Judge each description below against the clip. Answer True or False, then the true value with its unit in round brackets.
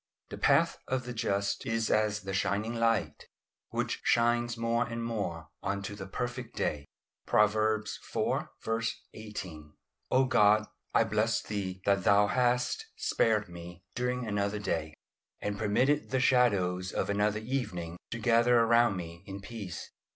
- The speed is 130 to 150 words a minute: True (145 wpm)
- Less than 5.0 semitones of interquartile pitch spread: True (3.1 semitones)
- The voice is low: True (110 Hz)